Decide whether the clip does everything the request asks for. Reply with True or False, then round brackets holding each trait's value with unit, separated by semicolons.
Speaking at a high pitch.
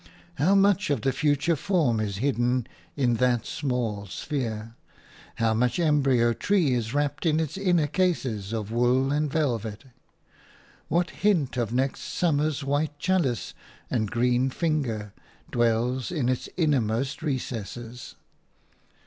False (130 Hz)